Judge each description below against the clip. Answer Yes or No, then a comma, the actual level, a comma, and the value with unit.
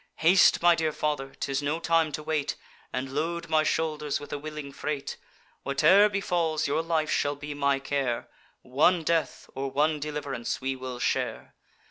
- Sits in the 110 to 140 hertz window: No, medium, 150 Hz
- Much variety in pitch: No, average, 2.7 semitones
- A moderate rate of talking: Yes, average, 165 wpm